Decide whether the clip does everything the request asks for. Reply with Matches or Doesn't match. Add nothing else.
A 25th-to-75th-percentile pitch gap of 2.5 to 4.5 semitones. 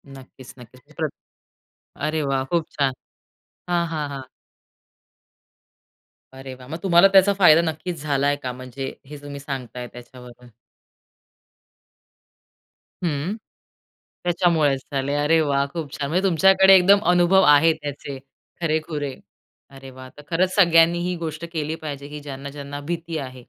Matches